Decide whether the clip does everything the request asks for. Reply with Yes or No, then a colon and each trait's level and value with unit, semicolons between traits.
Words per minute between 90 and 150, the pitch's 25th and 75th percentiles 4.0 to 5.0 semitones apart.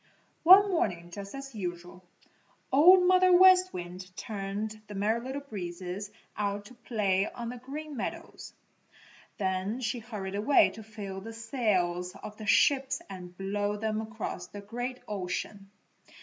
Yes: average, 145 wpm; average, 4.5 semitones